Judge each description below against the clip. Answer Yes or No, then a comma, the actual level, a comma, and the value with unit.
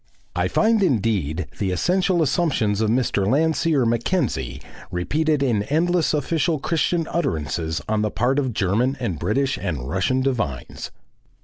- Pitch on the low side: Yes, low, 125 Hz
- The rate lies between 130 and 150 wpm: Yes, slow, 135 wpm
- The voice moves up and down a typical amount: No, wide, 8.2 semitones